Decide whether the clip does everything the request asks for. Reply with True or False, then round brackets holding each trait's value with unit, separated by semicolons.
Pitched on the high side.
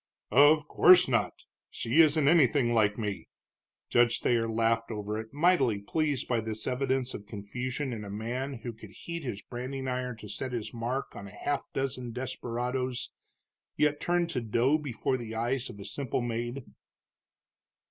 False (125 Hz)